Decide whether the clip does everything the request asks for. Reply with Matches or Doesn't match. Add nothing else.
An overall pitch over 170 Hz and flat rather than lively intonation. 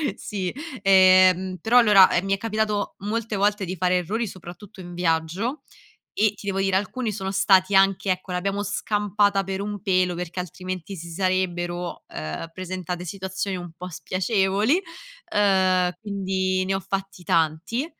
Matches